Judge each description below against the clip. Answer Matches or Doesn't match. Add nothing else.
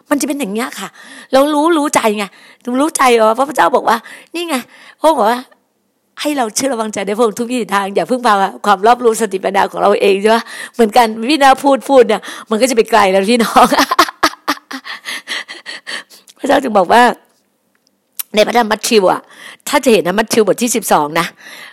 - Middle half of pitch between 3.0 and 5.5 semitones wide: Matches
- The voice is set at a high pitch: Matches